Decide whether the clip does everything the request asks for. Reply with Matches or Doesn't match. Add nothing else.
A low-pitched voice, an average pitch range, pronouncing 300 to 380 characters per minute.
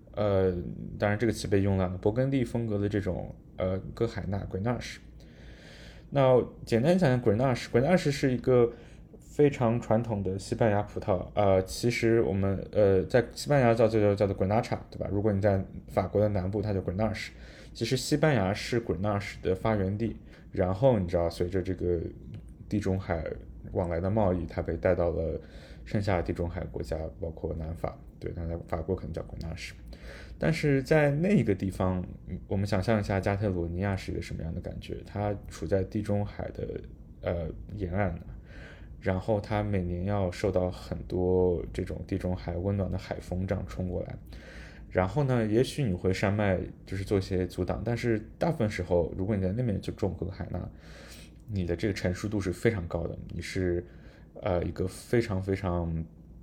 Matches